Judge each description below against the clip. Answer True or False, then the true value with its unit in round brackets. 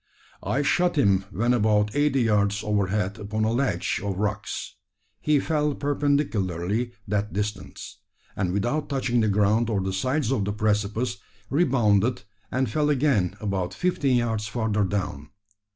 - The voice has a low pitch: True (110 Hz)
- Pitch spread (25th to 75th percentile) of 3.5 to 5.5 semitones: True (4.3 semitones)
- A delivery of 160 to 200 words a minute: False (145 wpm)